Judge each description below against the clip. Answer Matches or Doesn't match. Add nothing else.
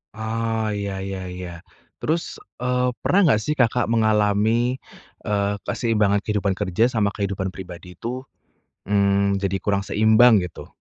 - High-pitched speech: Doesn't match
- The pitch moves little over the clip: Matches